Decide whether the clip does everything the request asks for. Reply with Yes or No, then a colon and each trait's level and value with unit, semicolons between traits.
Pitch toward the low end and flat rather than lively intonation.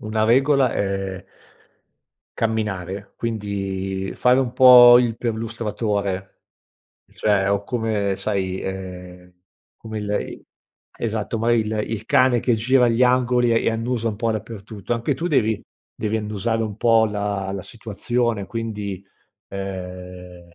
No: low, 110 Hz; average, 3.1 semitones